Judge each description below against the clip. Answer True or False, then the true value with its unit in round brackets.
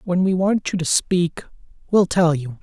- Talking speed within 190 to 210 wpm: True (205 wpm)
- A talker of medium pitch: True (175 Hz)